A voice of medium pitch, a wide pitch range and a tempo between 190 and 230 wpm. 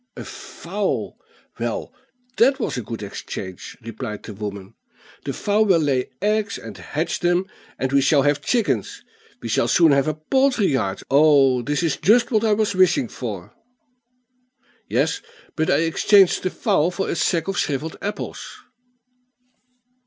No: medium, 155 Hz; wide, 7.9 semitones; average, 155 wpm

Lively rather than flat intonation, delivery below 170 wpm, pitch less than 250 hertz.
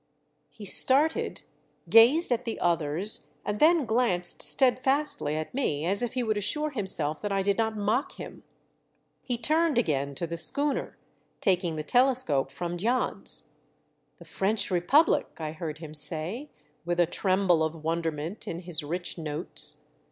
Yes: wide, 7.1 semitones; average, 150 wpm; high, 190 Hz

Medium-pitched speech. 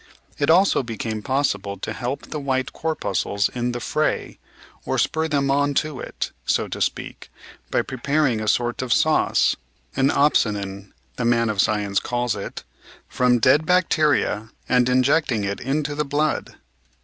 No: low, 125 Hz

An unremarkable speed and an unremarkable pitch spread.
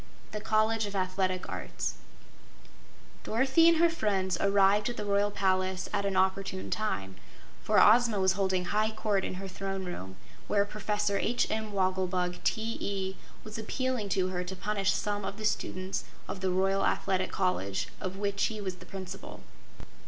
No: average, 165 wpm; narrow, 2.1 semitones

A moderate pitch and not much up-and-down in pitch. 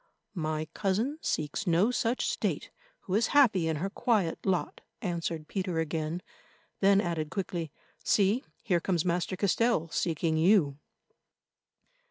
No: medium, 180 Hz; average, 3.8 semitones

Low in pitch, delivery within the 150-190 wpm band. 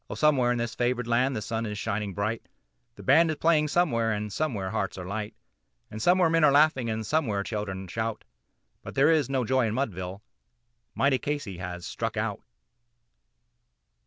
Yes: low, 115 Hz; average, 180 wpm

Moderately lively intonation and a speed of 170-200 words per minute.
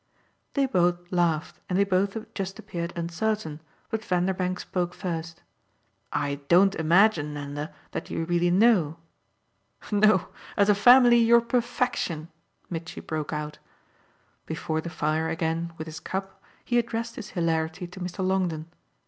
No: average, 3.9 semitones; average, 140 wpm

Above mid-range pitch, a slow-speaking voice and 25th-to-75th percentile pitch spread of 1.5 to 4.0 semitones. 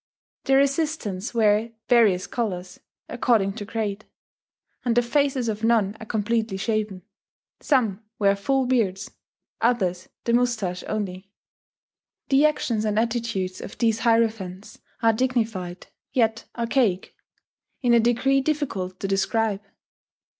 Yes: high, 225 Hz; slow, 120 wpm; average, 3.5 semitones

